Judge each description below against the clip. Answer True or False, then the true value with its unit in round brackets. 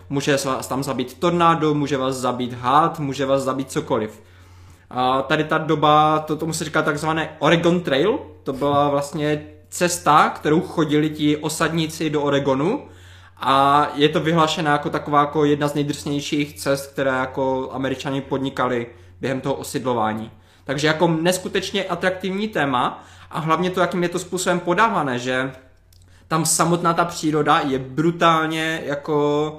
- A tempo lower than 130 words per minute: False (150 wpm)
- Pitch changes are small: False (3.3 semitones)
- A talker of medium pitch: True (145 Hz)